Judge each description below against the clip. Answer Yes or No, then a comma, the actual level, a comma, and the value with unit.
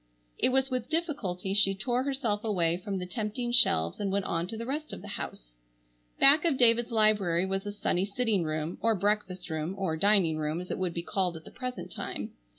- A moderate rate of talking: No, fast, 210 wpm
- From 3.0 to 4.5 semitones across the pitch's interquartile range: No, average, 5.1 semitones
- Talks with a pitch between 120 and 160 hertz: No, high, 200 Hz